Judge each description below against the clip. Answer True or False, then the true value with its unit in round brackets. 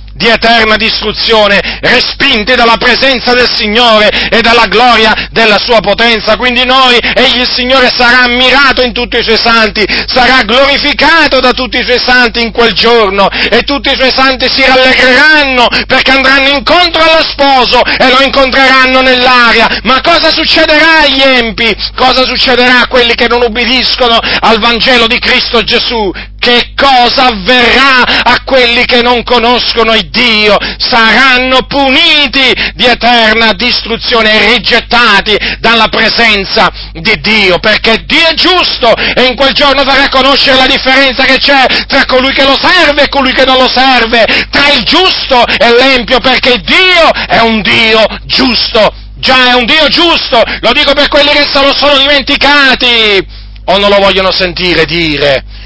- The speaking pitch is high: True (250 Hz)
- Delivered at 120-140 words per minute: False (155 wpm)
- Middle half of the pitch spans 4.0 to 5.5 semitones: False (2.9 semitones)